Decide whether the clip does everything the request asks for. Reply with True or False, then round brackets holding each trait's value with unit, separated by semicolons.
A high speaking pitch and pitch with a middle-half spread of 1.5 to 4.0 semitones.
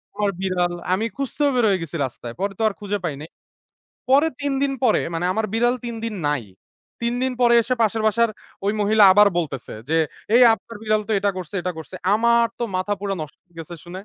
False (205 Hz; 4.6 semitones)